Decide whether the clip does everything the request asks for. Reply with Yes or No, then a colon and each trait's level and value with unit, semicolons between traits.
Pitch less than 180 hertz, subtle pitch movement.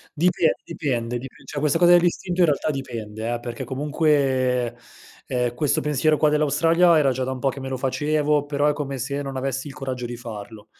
No: low, 135 Hz; average, 3.2 semitones